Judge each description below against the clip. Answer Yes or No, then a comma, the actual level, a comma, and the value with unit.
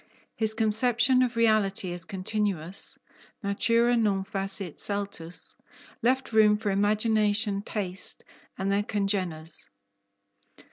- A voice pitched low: No, high, 205 Hz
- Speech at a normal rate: No, slow, 100 wpm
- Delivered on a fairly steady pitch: Yes, narrow, 2.3 semitones